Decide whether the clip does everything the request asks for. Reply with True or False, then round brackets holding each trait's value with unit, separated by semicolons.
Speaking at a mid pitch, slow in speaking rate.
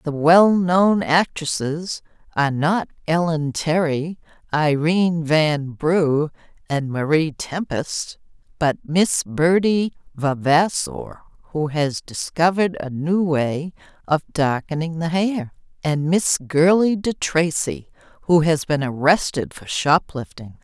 True (160 Hz; 115 wpm)